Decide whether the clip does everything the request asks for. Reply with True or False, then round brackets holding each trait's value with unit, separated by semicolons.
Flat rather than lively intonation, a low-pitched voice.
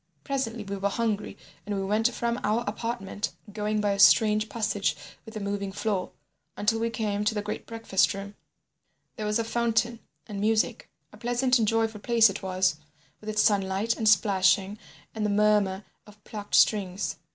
False (2.0 semitones; 210 Hz)